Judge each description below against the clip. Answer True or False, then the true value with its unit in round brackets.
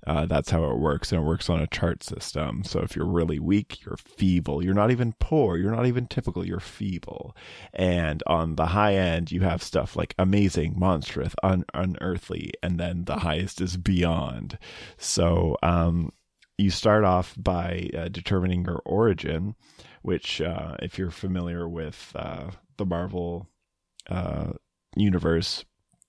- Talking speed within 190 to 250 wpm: False (160 wpm)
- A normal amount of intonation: False (2.2 semitones)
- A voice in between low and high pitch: False (90 Hz)